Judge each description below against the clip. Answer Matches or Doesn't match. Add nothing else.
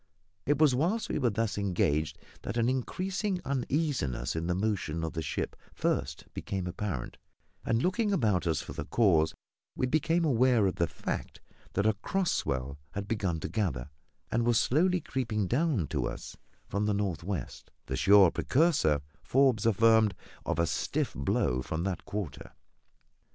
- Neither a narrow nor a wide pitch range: Doesn't match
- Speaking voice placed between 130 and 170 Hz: Doesn't match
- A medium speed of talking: Matches